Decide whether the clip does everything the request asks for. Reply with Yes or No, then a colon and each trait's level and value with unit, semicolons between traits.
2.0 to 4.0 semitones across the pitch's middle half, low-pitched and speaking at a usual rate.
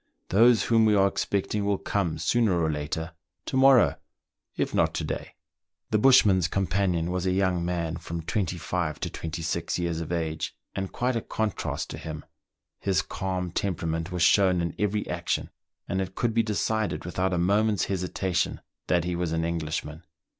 Yes: average, 3.3 semitones; very low, 90 Hz; average, 180 wpm